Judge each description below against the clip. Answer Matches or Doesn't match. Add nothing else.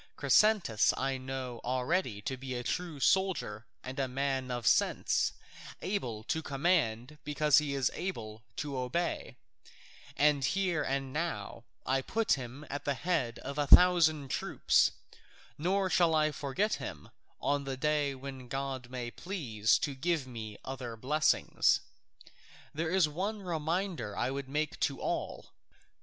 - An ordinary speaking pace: Matches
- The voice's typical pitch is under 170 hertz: Matches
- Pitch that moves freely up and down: Doesn't match